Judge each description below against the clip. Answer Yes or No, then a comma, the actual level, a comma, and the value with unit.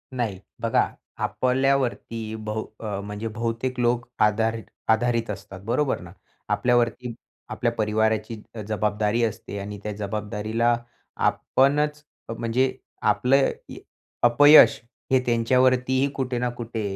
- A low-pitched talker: Yes, low, 115 Hz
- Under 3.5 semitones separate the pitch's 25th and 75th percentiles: Yes, average, 2.8 semitones